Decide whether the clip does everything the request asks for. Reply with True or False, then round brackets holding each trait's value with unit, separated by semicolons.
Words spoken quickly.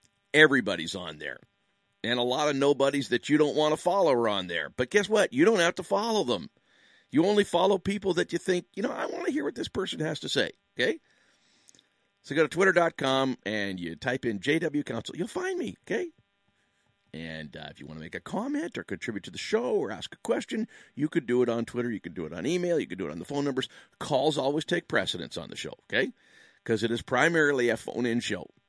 True (240 wpm)